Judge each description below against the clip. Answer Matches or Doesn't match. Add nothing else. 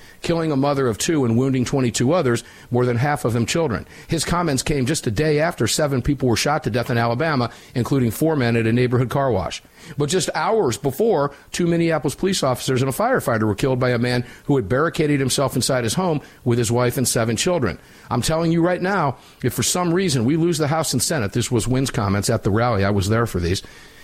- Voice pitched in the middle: Doesn't match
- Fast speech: Matches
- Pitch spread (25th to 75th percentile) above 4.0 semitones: Matches